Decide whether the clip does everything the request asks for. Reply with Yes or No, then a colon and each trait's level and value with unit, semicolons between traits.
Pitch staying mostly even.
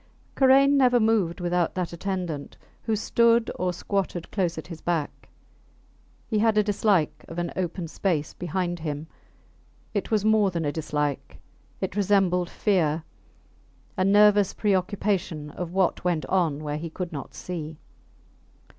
No: average, 3.9 semitones